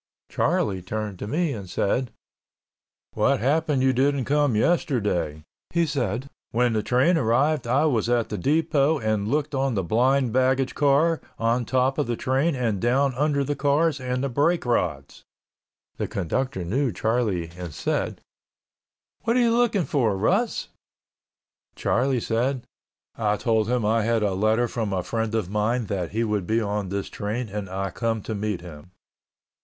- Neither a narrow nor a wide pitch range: Yes, average, 4.7 semitones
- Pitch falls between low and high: No, low, 120 Hz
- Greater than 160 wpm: Yes, average, 170 wpm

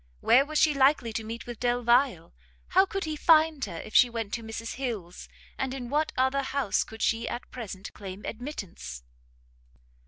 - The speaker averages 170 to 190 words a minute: Yes, average, 180 wpm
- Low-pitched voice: No, high, 240 Hz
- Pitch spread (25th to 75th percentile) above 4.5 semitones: No, average, 4.0 semitones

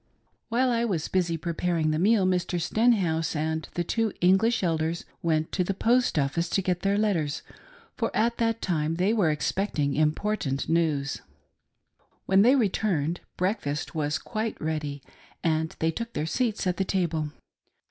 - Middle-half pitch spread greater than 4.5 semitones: Yes, average, 5.0 semitones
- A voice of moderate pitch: Yes, medium, 175 Hz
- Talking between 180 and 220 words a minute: No, average, 155 wpm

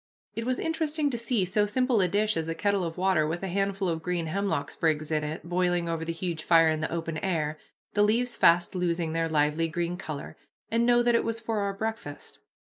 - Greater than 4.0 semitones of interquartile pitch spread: Yes, average, 4.6 semitones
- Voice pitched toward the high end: No, medium, 180 Hz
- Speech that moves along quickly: Yes, fast, 230 wpm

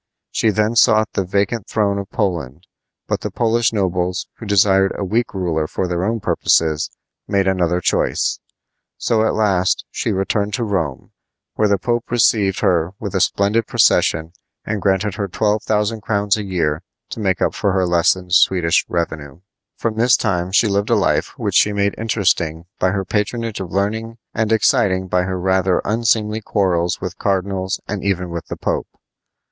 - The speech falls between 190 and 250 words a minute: No, average, 175 wpm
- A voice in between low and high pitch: No, low, 100 Hz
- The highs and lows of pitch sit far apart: No, average, 2.9 semitones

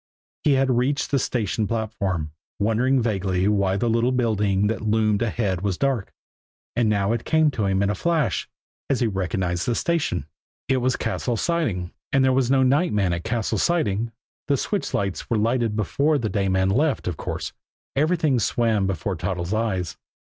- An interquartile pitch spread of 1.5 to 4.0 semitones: No, average, 4.9 semitones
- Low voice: Yes, low, 110 Hz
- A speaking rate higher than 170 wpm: Yes, average, 180 wpm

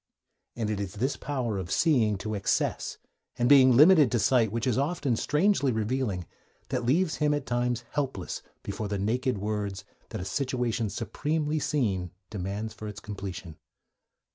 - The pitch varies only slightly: No, average, 4.8 semitones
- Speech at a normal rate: Yes, average, 160 wpm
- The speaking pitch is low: Yes, low, 120 Hz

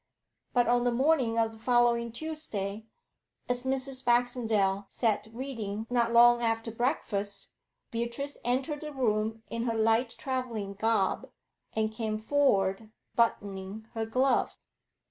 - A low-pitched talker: No, high, 230 Hz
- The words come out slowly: Yes, slow, 125 wpm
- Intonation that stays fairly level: Yes, narrow, 2.3 semitones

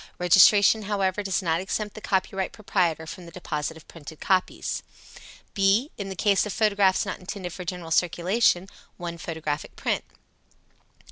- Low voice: No, medium, 185 Hz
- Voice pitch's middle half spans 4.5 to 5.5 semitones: No, average, 2.9 semitones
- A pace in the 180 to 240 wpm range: No, average, 150 wpm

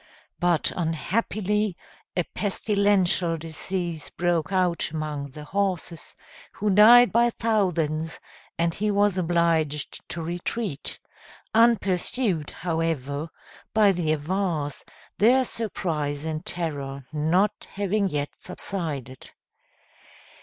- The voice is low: No, medium, 175 Hz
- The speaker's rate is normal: No, slow, 95 wpm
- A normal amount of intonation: Yes, average, 4.5 semitones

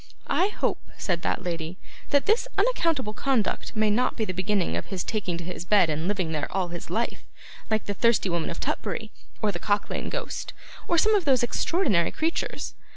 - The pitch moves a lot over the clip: Yes, wide, 6.9 semitones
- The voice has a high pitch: Yes, high, 205 Hz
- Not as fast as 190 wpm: No, average, 200 wpm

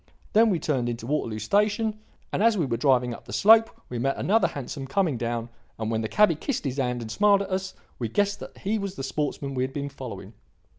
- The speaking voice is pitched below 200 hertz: Yes, medium, 140 Hz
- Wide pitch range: Yes, wide, 8.7 semitones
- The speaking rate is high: Yes, fast, 235 wpm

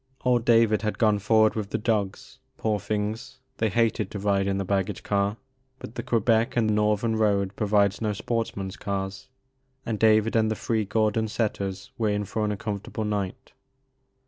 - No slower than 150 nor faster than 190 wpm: Yes, average, 180 wpm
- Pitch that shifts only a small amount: Yes, narrow, 1.8 semitones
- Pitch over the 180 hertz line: No, low, 105 Hz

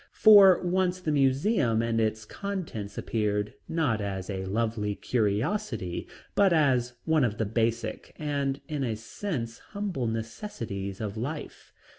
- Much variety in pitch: Yes, wide, 6.8 semitones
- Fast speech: No, slow, 135 wpm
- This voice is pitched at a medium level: No, low, 115 Hz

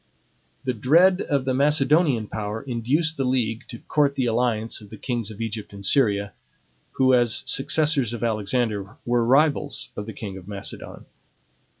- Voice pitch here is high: No, low, 120 Hz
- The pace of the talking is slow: No, average, 165 wpm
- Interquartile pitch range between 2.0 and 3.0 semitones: No, average, 4.3 semitones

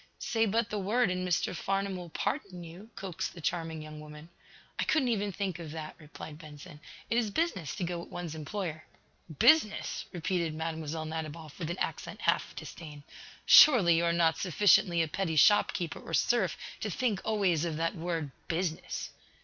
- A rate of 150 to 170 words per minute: No, average, 180 wpm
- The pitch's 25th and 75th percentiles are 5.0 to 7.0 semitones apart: No, average, 3.7 semitones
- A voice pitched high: No, medium, 170 Hz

